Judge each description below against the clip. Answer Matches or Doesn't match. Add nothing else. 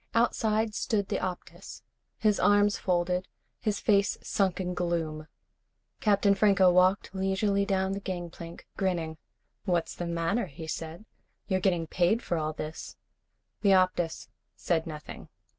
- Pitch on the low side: Doesn't match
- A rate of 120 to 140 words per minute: Matches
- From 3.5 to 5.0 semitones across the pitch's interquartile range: Doesn't match